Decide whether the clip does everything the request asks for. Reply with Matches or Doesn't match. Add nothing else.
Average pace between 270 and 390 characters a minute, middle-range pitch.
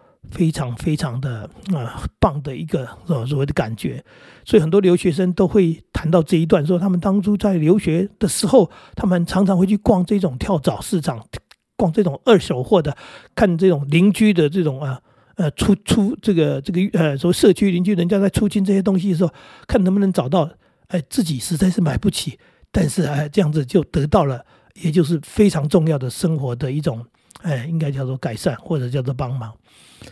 Matches